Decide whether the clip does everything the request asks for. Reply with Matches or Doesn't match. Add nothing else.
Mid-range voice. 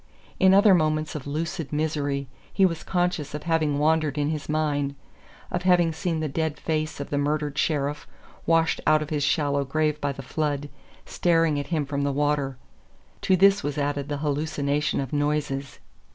Matches